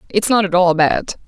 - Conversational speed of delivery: No, fast, 235 wpm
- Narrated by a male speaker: No, female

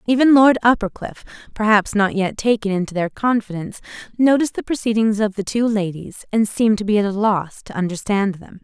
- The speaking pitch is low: No, high, 210 Hz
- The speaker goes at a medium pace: Yes, average, 190 wpm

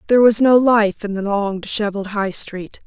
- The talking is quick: Yes, fast, 210 wpm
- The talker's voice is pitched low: No, high, 210 Hz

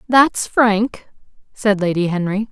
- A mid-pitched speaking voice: No, high, 210 Hz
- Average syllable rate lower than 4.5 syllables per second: Yes, 3.7 syllables/s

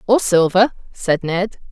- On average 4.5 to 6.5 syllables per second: No, 3.8 syllables/s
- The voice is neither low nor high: No, high, 195 Hz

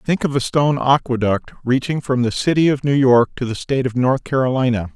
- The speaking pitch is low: Yes, low, 130 Hz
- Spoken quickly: Yes, fast, 220 wpm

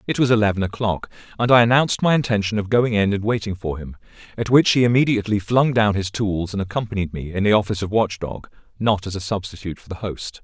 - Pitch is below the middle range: Yes, low, 105 Hz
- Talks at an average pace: No, fast, 225 wpm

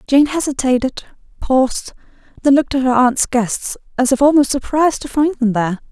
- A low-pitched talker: No, very high, 265 Hz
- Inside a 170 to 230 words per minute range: No, average, 160 wpm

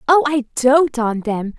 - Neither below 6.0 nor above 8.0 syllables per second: No, 4.0 syllables/s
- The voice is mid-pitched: No, very high, 265 Hz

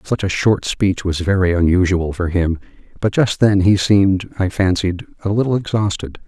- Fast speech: No, average, 180 wpm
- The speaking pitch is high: No, very low, 95 Hz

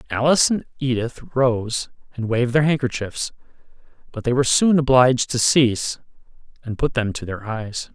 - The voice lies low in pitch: Yes, low, 125 Hz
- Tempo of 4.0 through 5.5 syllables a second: Yes, 5.2 syllables/s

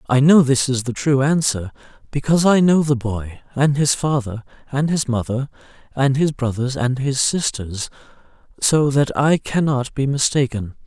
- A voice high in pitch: No, low, 135 Hz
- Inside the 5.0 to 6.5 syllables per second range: No, 4.6 syllables/s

